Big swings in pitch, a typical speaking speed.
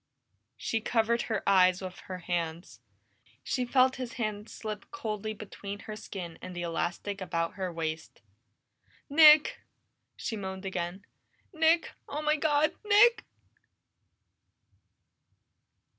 No: wide, 6.0 semitones; slow, 115 wpm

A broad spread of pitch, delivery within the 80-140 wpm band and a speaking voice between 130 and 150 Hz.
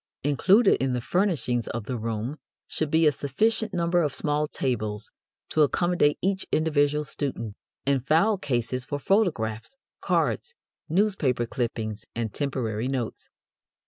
Yes: wide, 6.0 semitones; slow, 135 wpm; medium, 140 Hz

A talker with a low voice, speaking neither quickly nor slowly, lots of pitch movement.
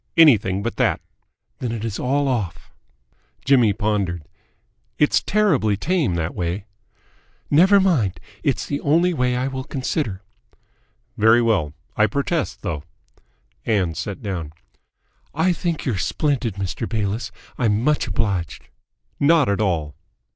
No: low, 115 Hz; slow, 130 wpm; wide, 6.5 semitones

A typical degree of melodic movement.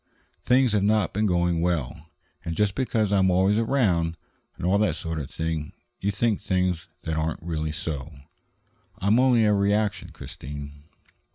Yes: average, 4.5 semitones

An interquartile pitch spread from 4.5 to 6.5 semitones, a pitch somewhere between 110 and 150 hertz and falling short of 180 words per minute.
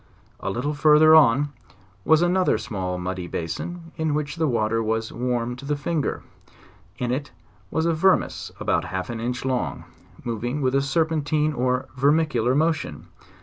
Yes: average, 5.2 semitones; low, 135 Hz; average, 155 wpm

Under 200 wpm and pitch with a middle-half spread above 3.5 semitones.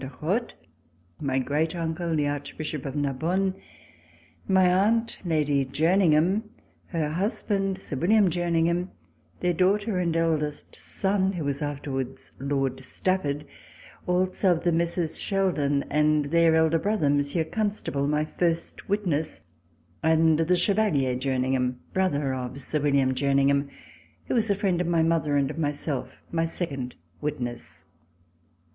Yes: slow, 135 wpm; average, 4.3 semitones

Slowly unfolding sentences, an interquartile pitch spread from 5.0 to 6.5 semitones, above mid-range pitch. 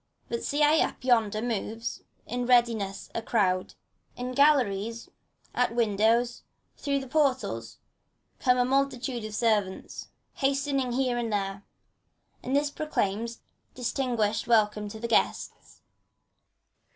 No: slow, 125 wpm; average, 3.5 semitones; high, 235 Hz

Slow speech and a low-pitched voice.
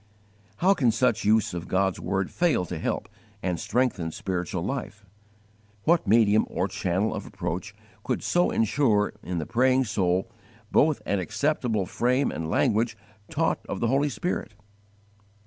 No: average, 145 wpm; low, 110 Hz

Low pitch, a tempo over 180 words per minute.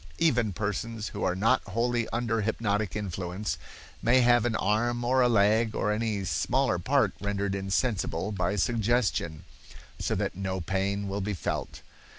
No: low, 105 Hz; average, 155 wpm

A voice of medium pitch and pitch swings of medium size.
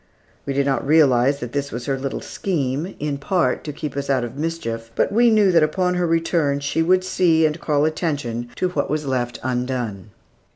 Yes: medium, 145 Hz; average, 4.1 semitones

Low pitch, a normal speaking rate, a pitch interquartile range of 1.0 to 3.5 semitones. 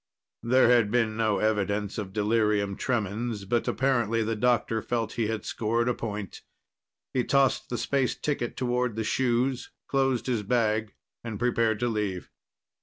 Yes: low, 115 Hz; average, 155 wpm; narrow, 2.5 semitones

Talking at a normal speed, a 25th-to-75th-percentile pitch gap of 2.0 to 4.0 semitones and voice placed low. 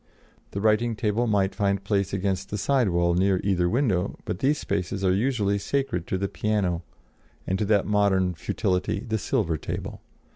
Yes: average, 175 wpm; narrow, 2.5 semitones; low, 100 Hz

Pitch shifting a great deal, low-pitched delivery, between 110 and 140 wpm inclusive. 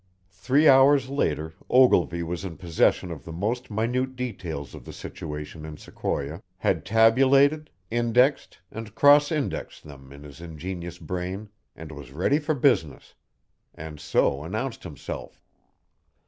Yes: wide, 8.3 semitones; very low, 95 Hz; slow, 135 wpm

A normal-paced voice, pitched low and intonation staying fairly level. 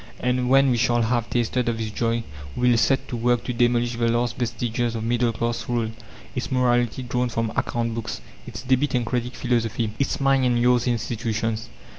Yes: average, 195 wpm; low, 120 Hz; narrow, 1.2 semitones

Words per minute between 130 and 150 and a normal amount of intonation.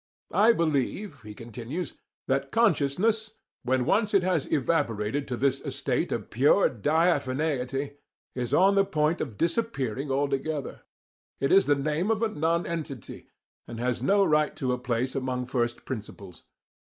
Yes: average, 145 wpm; average, 4.9 semitones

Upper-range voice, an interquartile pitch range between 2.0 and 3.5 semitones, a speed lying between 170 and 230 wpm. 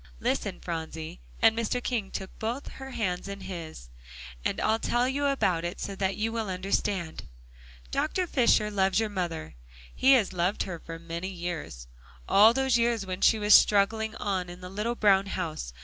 No: high, 195 Hz; average, 4.1 semitones; average, 180 wpm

